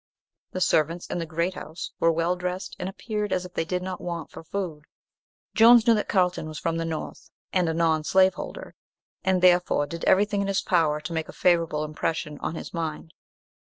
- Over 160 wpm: Yes, average, 200 wpm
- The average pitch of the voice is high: No, medium, 175 Hz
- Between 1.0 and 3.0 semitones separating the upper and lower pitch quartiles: Yes, narrow, 2.5 semitones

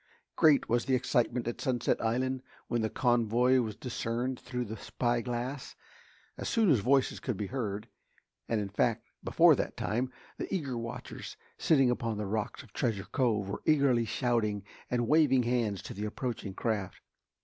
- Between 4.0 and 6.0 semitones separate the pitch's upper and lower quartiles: No, average, 2.7 semitones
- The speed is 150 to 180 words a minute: Yes, average, 165 wpm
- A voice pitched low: Yes, low, 120 Hz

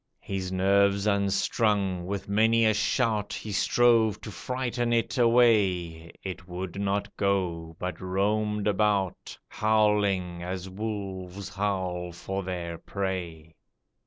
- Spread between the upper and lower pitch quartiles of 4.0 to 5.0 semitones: No, narrow, 2.5 semitones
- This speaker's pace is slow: Yes, slow, 115 wpm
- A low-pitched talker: Yes, low, 100 Hz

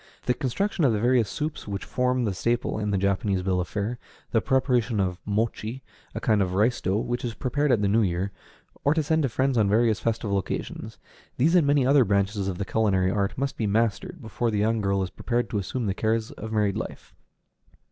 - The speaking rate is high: Yes, fast, 220 wpm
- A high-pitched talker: No, low, 110 Hz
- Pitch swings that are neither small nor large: Yes, average, 4.0 semitones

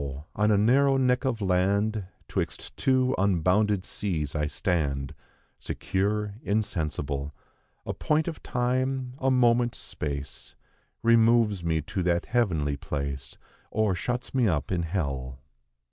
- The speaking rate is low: Yes, slow, 125 wpm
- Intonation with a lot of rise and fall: Yes, wide, 7.3 semitones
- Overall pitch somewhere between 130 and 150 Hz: No, low, 100 Hz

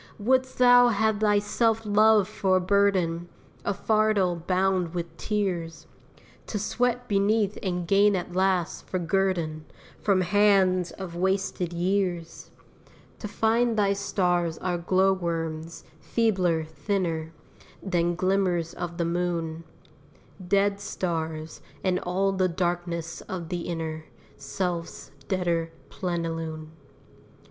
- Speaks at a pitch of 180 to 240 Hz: Yes, medium, 185 Hz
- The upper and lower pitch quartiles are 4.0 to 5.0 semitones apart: No, average, 3.0 semitones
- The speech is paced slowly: Yes, slow, 120 wpm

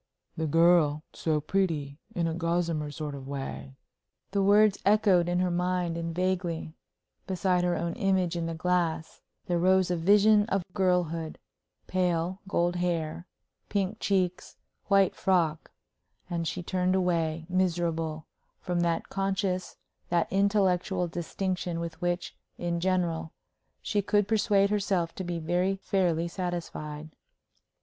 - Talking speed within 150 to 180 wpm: No, slow, 135 wpm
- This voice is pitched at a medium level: Yes, medium, 175 Hz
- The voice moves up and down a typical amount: No, narrow, 2.3 semitones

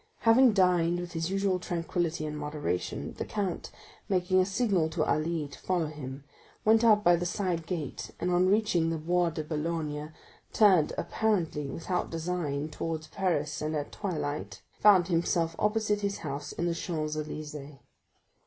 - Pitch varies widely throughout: No, average, 3.4 semitones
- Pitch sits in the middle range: Yes, medium, 170 Hz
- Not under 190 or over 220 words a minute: No, average, 160 wpm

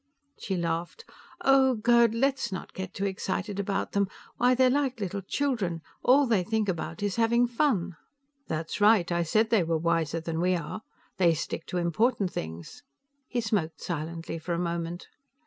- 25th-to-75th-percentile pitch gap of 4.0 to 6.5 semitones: Yes, wide, 5.5 semitones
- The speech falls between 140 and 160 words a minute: No, average, 170 wpm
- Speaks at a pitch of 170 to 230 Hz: Yes, high, 190 Hz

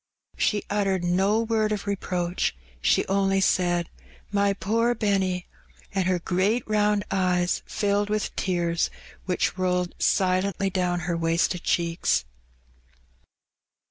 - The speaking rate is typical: No, slow, 115 wpm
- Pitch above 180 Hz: Yes, high, 190 Hz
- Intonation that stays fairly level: Yes, narrow, 2.3 semitones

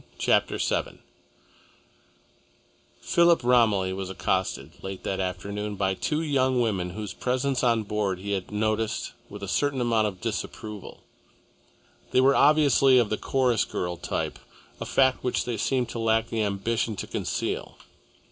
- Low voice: Yes, low, 110 Hz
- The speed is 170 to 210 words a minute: No, average, 145 wpm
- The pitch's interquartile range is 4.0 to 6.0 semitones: Yes, average, 4.5 semitones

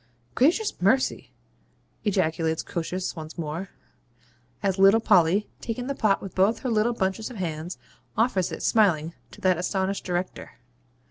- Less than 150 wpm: Yes, average, 140 wpm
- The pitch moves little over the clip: No, average, 4.1 semitones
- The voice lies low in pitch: No, high, 190 Hz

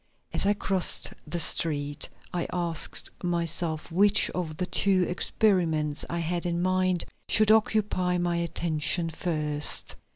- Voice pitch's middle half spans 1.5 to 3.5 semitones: Yes, narrow, 2.4 semitones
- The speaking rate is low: Yes, slow, 130 wpm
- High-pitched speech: No, medium, 175 Hz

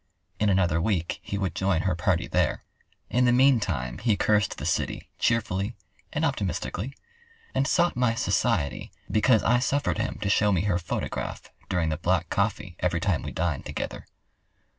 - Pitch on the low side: Yes, low, 100 Hz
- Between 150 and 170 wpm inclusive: Yes, average, 165 wpm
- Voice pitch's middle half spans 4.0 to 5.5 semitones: Yes, average, 4.6 semitones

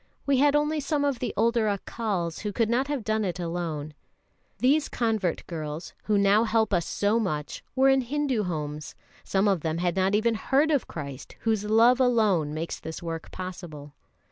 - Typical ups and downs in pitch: No, wide, 6.2 semitones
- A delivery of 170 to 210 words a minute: Yes, average, 185 wpm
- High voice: Yes, high, 210 Hz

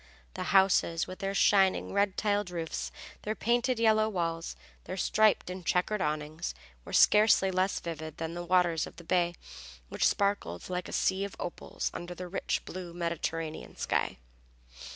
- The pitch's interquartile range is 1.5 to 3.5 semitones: Yes, average, 2.9 semitones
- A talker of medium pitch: Yes, medium, 180 Hz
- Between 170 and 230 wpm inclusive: No, average, 160 wpm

